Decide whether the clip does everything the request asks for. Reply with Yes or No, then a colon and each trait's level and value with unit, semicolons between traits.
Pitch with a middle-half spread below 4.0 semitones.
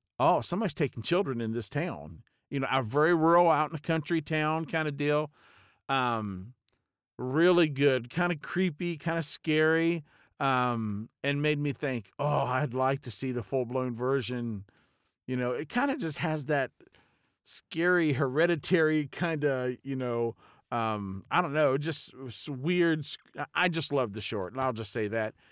No: average, 4.6 semitones